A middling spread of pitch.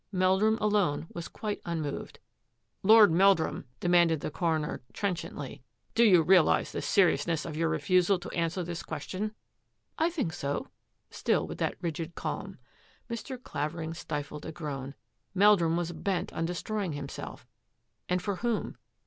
Yes: average, 3.8 semitones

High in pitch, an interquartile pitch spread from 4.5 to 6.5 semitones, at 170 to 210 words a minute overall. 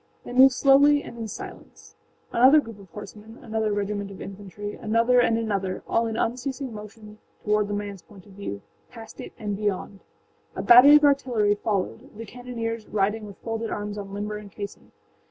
No: high, 215 Hz; narrow, 2.5 semitones; average, 175 wpm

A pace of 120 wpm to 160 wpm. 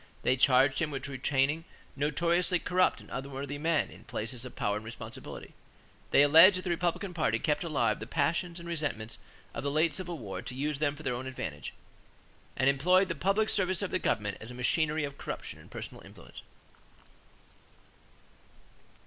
No: average, 175 wpm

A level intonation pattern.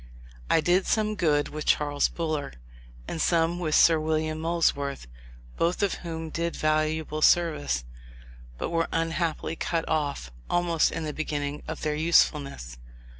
Yes: narrow, 2.0 semitones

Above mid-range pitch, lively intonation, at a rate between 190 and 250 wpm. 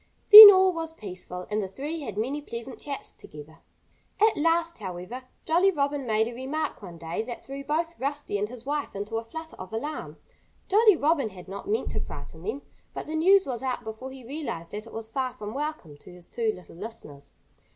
Yes: very high, 255 Hz; wide, 6.9 semitones; fast, 205 wpm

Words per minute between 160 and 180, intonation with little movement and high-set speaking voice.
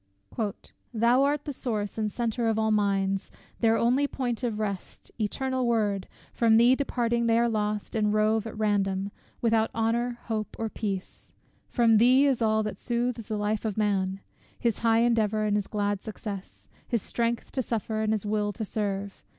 Yes: average, 175 wpm; narrow, 2.2 semitones; high, 220 Hz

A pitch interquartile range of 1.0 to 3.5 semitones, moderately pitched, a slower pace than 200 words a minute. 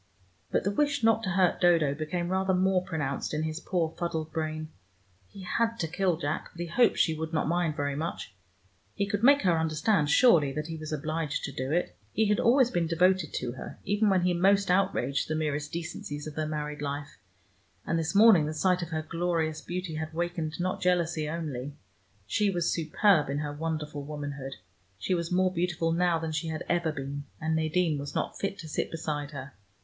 No: average, 3.1 semitones; medium, 165 Hz; fast, 205 wpm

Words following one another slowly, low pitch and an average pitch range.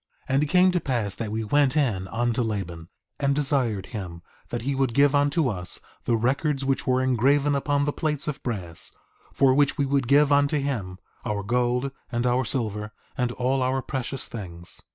No: average, 195 wpm; low, 130 Hz; average, 4.2 semitones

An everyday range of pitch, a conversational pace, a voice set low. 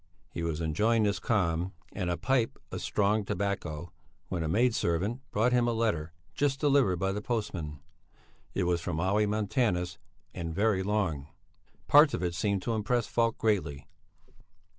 Yes: average, 4.8 semitones; average, 160 wpm; low, 100 Hz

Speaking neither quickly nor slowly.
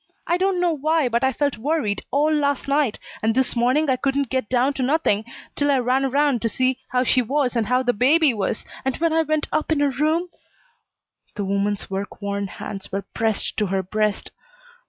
No: fast, 215 wpm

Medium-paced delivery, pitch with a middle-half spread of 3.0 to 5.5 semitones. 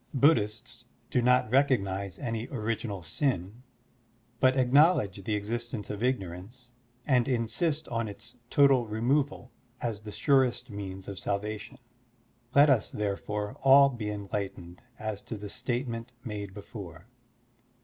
No: slow, 130 wpm; average, 3.8 semitones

